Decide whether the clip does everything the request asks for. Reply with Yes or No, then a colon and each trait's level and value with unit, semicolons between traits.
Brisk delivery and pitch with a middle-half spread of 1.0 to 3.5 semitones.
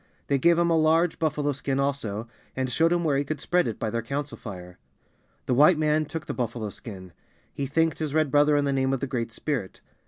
No: fast, 230 wpm; average, 4.4 semitones